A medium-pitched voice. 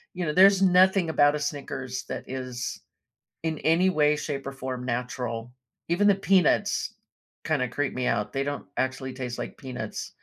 Yes: medium, 145 Hz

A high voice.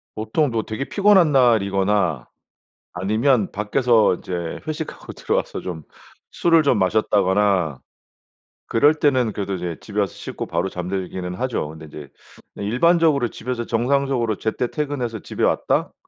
No: low, 110 Hz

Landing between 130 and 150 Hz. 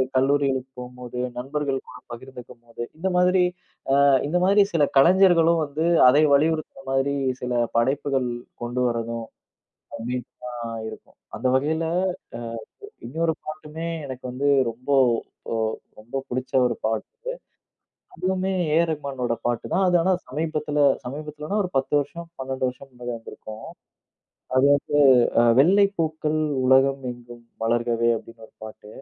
Yes: low, 135 Hz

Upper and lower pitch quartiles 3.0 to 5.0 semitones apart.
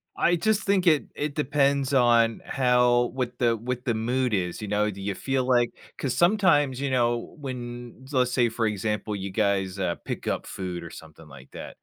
Yes: average, 4.1 semitones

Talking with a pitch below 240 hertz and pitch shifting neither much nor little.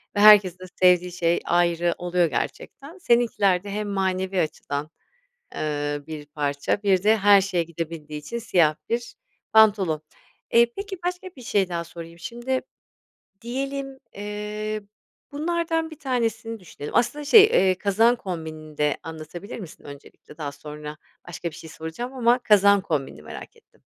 No: high, 190 Hz; wide, 6.3 semitones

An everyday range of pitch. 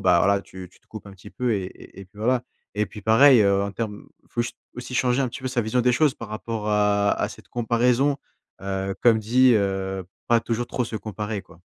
Yes: average, 3.4 semitones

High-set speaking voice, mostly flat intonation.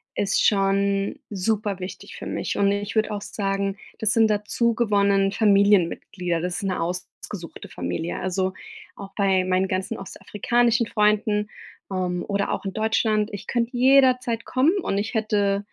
Yes: high, 200 Hz; narrow, 2.3 semitones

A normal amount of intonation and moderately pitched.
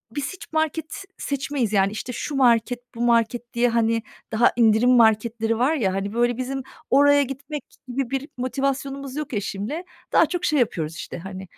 No: average, 3.6 semitones; high, 245 Hz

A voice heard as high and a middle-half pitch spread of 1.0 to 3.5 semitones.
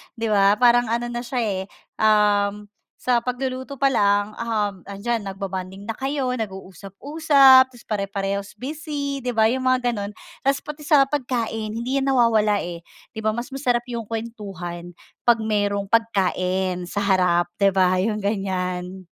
No: high, 220 Hz; average, 4.2 semitones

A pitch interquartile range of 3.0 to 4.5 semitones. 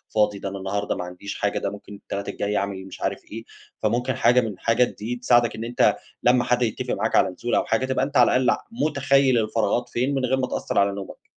Yes: average, 3.7 semitones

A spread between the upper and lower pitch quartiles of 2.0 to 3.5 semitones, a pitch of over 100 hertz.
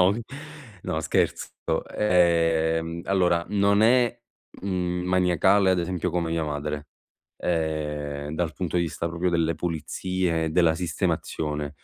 No: narrow, 2.5 semitones; very low, 85 Hz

